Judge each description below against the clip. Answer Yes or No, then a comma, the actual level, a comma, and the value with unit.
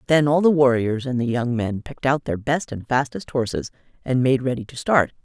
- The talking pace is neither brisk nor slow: No, fast, 230 wpm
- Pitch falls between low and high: No, low, 130 Hz